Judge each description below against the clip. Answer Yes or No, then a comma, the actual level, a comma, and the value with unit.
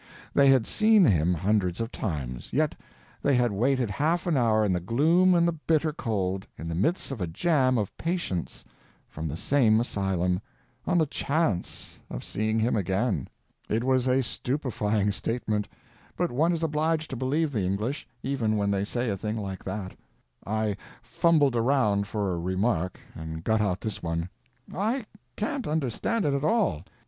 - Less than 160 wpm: No, average, 175 wpm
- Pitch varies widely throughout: Yes, wide, 7.2 semitones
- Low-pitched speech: Yes, low, 115 Hz